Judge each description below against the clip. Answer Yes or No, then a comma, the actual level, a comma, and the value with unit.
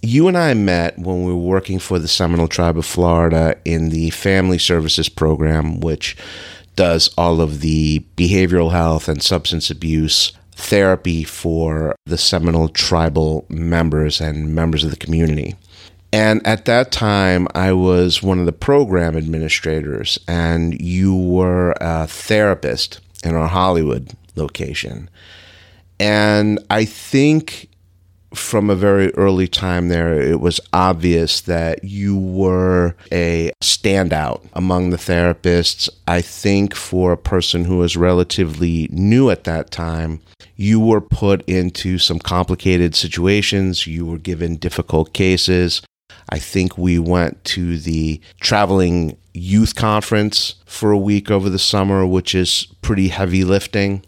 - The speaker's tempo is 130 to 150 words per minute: Yes, average, 140 wpm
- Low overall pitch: Yes, very low, 90 Hz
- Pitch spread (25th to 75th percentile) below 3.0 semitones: Yes, narrow, 2.6 semitones